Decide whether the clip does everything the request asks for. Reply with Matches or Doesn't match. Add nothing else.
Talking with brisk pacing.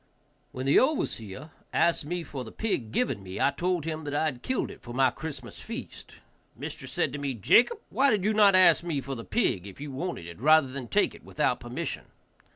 Matches